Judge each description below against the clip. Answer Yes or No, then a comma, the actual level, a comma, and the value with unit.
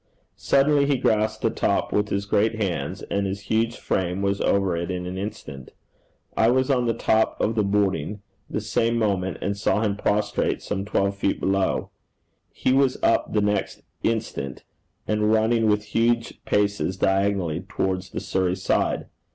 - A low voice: Yes, low, 105 Hz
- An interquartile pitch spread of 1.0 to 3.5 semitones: Yes, narrow, 2.5 semitones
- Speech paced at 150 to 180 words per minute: Yes, average, 165 wpm